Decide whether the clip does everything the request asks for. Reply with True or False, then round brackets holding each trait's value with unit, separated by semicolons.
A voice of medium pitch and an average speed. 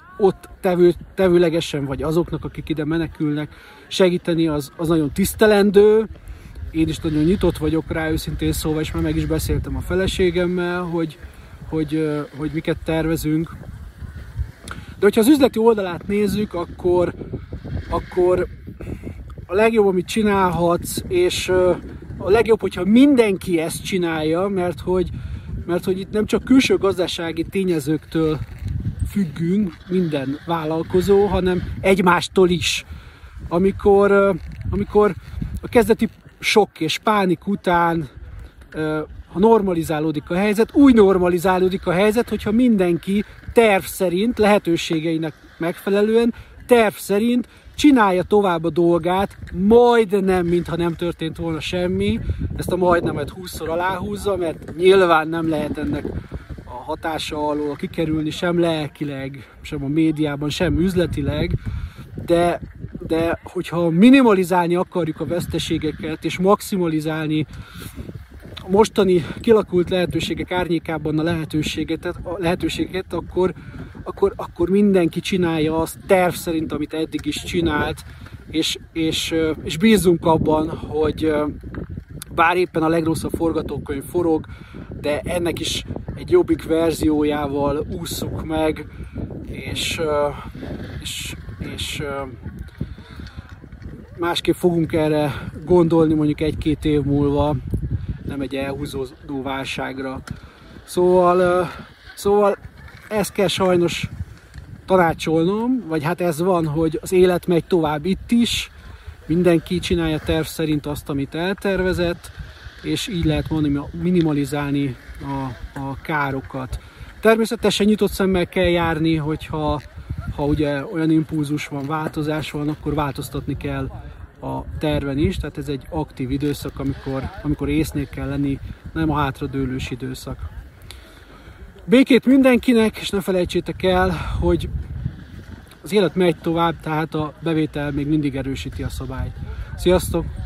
True (165 Hz; 115 wpm)